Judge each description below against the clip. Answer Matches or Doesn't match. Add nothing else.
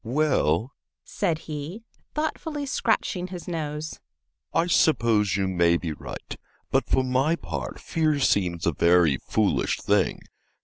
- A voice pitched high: Doesn't match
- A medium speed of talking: Doesn't match